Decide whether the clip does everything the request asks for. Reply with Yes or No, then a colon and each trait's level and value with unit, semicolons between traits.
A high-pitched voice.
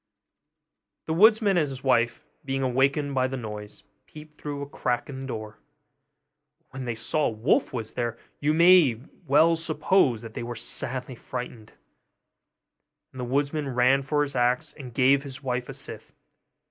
No: low, 135 Hz